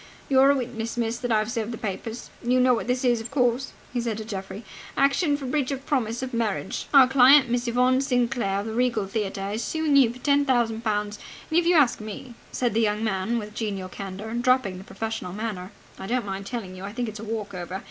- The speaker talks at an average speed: No, fast, 235 wpm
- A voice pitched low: No, high, 230 Hz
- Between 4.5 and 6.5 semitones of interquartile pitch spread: No, average, 3.3 semitones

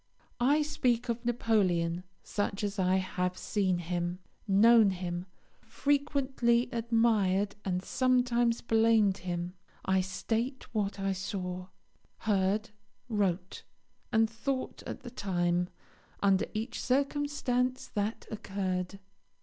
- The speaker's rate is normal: No, slow, 110 wpm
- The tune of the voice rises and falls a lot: No, average, 4.3 semitones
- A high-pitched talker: Yes, high, 210 Hz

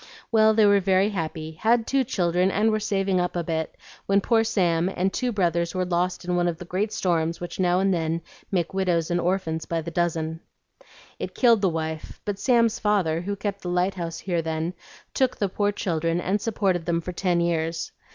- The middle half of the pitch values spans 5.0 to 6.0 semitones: No, average, 3.2 semitones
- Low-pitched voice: No, medium, 180 Hz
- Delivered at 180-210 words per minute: Yes, fast, 205 wpm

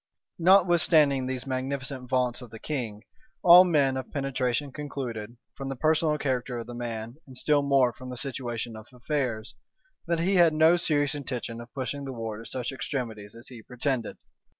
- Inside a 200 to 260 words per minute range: No, average, 175 wpm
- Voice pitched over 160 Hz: No, low, 130 Hz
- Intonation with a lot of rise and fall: No, average, 3.3 semitones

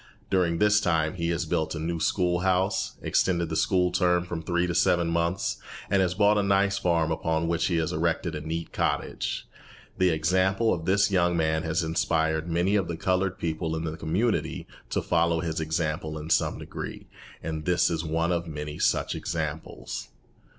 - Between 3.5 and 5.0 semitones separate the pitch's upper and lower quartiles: No, narrow, 2.4 semitones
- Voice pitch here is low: Yes, very low, 85 Hz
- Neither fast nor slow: Yes, average, 185 wpm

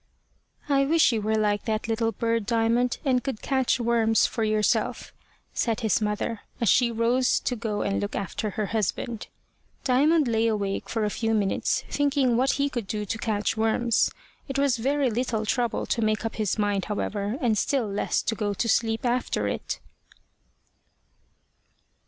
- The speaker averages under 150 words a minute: No, average, 170 wpm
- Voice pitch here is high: Yes, high, 225 Hz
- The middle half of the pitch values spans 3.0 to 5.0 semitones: No, narrow, 2.5 semitones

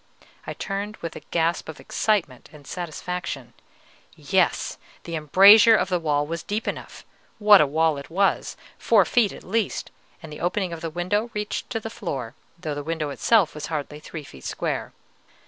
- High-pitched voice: No, medium, 170 Hz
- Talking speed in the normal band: Yes, average, 180 wpm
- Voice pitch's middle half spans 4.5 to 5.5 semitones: Yes, average, 5.1 semitones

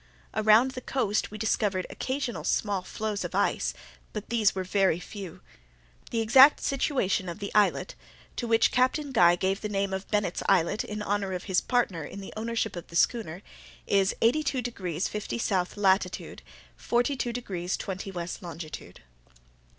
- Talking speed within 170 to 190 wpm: No, average, 160 wpm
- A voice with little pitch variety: No, average, 3.8 semitones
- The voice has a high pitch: Yes, high, 205 Hz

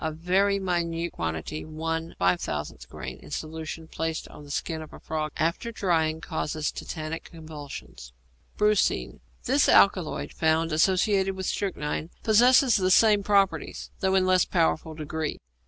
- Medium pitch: Yes, medium, 165 Hz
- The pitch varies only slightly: No, average, 3.4 semitones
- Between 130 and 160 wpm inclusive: Yes, average, 140 wpm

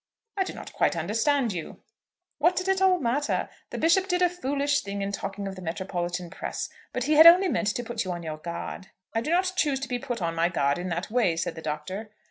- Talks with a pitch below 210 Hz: No, high, 225 Hz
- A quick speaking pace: Yes, fast, 245 wpm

